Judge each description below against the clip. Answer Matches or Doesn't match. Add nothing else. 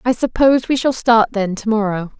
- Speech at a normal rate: Doesn't match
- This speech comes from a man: Doesn't match